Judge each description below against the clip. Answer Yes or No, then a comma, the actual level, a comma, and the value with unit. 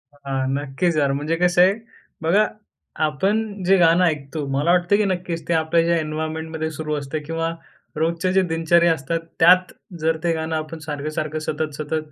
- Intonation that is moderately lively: No, narrow, 2.0 semitones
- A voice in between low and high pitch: Yes, medium, 160 Hz